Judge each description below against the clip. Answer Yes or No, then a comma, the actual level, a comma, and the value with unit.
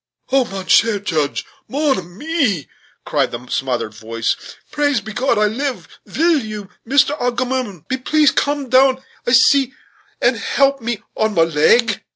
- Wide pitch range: Yes, wide, 6.0 semitones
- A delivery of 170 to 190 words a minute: No, average, 150 wpm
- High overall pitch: Yes, high, 240 Hz